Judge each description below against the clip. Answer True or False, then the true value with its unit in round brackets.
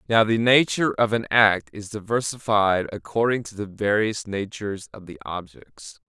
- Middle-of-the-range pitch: False (105 Hz)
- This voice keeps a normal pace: True (160 wpm)